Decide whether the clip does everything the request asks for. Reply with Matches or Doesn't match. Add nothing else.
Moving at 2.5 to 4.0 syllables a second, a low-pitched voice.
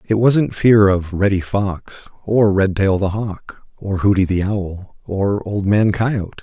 Matches